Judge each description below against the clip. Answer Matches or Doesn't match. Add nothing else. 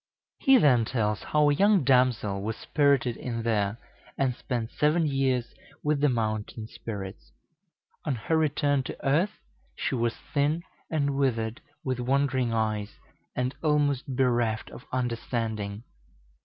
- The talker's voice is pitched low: Matches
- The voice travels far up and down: Doesn't match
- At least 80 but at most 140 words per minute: Matches